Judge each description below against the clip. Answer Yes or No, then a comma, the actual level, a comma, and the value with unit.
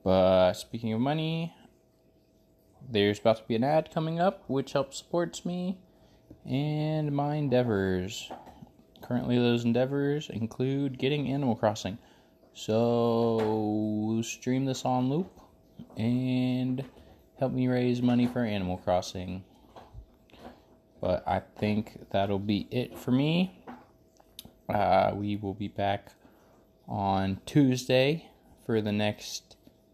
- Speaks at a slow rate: Yes, slow, 115 wpm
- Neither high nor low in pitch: No, low, 120 Hz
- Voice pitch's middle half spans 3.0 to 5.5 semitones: Yes, average, 4.5 semitones